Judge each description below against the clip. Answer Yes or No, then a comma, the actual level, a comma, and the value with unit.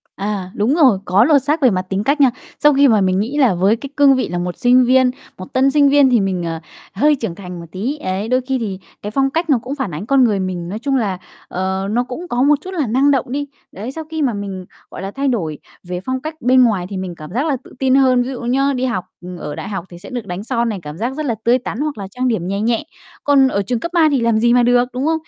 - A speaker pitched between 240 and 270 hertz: Yes, high, 245 Hz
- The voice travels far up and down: Yes, wide, 5.8 semitones